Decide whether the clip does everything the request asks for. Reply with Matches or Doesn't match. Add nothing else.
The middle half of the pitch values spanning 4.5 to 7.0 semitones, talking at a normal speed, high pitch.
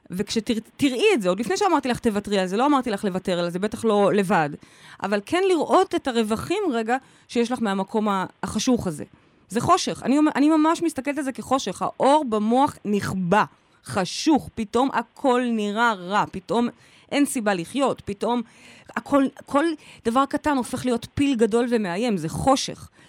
Doesn't match